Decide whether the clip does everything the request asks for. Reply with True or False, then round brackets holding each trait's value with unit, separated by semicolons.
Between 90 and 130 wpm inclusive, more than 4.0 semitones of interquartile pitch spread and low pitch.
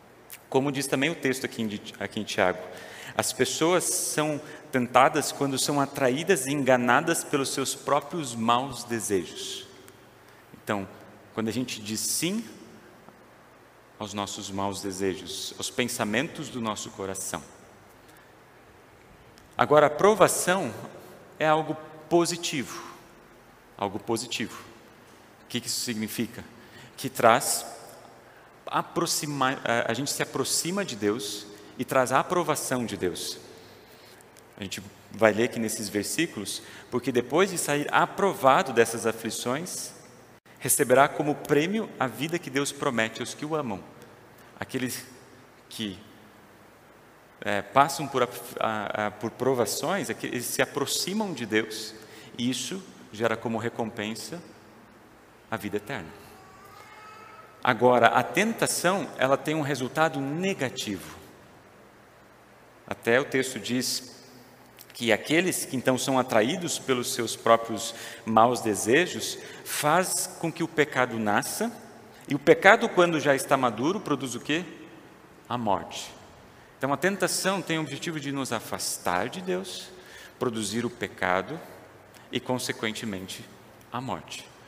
True (120 wpm; 5.1 semitones; 125 Hz)